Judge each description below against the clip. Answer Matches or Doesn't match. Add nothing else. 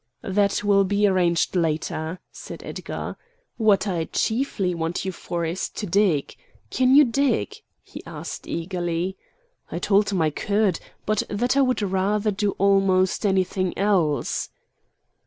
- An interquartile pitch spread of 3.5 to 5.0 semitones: Doesn't match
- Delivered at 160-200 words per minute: Doesn't match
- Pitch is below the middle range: Doesn't match